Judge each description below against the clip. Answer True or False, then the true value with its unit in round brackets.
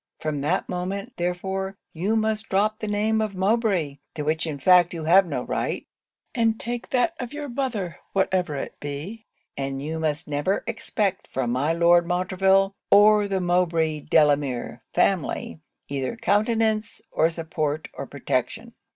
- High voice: False (180 Hz)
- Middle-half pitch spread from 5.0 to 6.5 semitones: True (5.4 semitones)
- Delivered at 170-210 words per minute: False (150 wpm)